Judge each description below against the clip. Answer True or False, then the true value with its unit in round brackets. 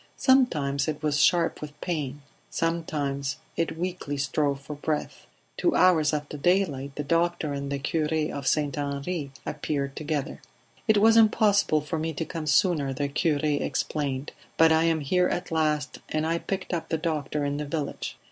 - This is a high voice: False (150 Hz)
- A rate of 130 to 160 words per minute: False (170 wpm)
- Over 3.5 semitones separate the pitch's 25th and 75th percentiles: False (2.8 semitones)